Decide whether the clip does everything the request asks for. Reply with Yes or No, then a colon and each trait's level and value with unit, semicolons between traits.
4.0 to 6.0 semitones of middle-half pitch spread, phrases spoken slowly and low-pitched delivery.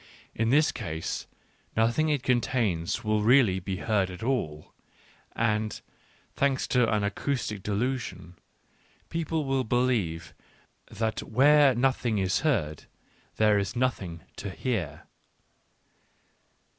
Yes: average, 5.1 semitones; slow, 110 wpm; low, 110 Hz